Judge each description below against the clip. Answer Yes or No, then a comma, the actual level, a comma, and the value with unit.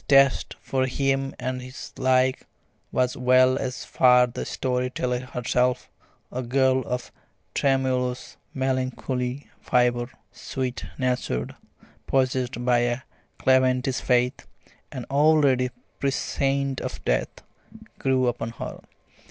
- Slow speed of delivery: Yes, slow, 115 wpm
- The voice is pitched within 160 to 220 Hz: No, low, 130 Hz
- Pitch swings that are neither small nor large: No, narrow, 1.0 semitones